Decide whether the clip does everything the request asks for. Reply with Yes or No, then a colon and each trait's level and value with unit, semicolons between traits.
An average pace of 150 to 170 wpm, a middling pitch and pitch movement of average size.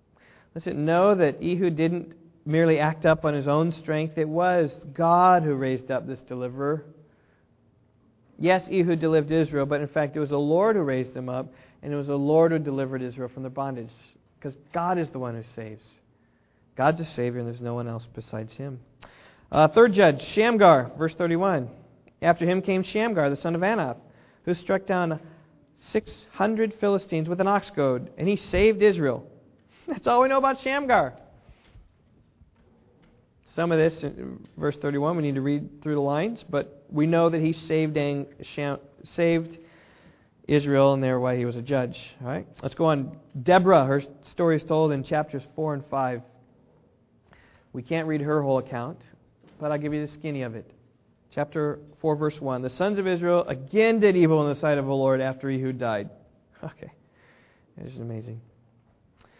No: average, 180 wpm; medium, 150 Hz; average, 4.3 semitones